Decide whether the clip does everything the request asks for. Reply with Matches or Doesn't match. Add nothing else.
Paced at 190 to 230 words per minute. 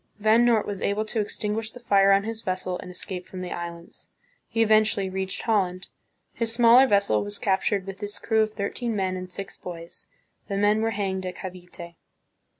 Matches